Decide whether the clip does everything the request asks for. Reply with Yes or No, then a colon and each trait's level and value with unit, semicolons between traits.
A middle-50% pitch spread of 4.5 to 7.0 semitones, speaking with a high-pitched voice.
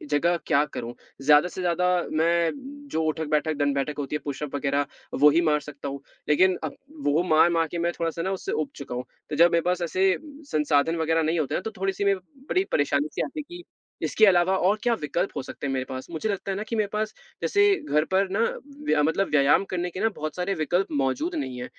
No: average, 4.8 semitones; medium, 165 Hz